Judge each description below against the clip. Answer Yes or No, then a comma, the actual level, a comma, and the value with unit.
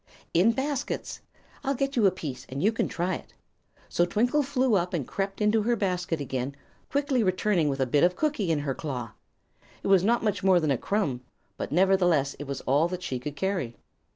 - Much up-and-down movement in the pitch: Yes, wide, 6.7 semitones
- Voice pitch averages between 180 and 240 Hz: Yes, medium, 185 Hz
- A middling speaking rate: No, fast, 210 wpm